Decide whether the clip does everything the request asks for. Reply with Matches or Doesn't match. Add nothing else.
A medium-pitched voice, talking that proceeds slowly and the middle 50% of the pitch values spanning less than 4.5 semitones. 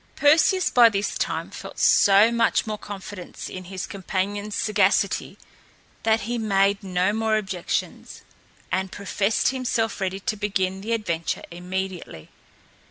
Doesn't match